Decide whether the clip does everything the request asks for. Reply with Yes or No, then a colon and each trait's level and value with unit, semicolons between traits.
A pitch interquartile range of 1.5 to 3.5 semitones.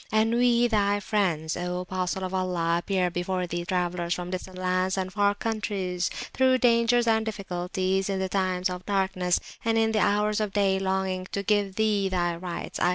Yes: narrow, 2.5 semitones